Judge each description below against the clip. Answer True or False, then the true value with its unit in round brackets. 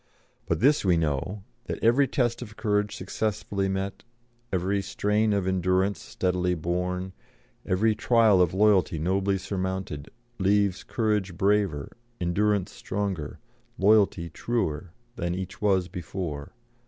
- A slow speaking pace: True (120 wpm)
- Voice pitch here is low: True (95 Hz)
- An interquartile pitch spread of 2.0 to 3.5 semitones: True (2.5 semitones)